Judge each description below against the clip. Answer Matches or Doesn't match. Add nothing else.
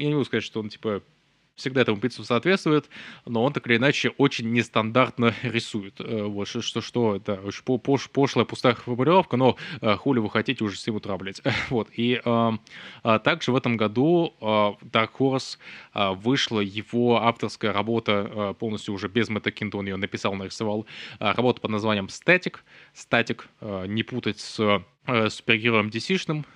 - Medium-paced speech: Doesn't match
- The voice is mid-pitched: Doesn't match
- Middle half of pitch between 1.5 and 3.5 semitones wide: Matches